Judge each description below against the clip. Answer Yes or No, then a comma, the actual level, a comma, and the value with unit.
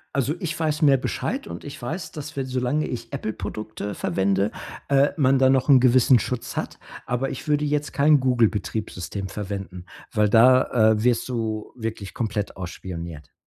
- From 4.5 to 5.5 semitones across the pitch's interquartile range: Yes, average, 4.8 semitones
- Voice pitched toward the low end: Yes, low, 120 Hz